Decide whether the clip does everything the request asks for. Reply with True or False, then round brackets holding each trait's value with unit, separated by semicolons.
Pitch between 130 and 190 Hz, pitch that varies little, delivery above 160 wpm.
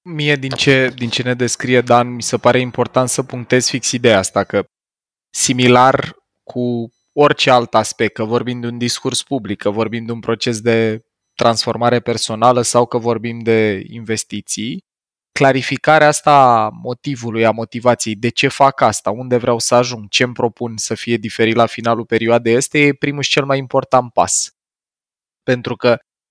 False (120 Hz; 2.0 semitones; 170 wpm)